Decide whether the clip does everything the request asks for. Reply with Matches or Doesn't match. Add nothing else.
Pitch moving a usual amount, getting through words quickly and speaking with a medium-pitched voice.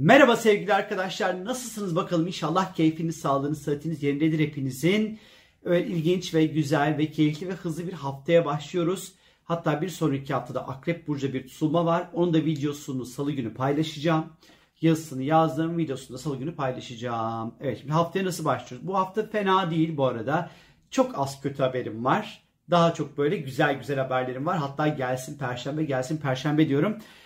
Matches